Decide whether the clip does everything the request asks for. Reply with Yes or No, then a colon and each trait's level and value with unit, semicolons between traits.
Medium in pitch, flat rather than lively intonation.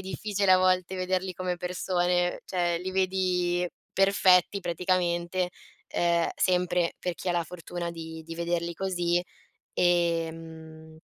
Yes: medium, 175 Hz; narrow, 1.3 semitones